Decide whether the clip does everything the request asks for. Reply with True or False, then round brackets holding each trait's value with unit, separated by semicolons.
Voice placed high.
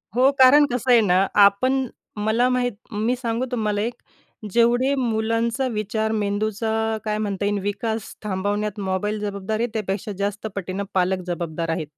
True (215 Hz)